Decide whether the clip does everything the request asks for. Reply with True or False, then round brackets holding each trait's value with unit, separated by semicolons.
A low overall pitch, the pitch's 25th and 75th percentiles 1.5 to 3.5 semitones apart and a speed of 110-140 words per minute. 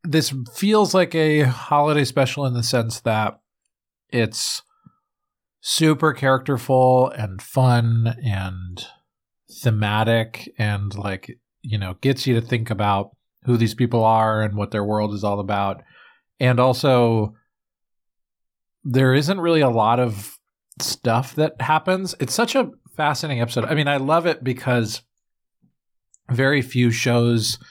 False (125 Hz; 4.4 semitones; 135 wpm)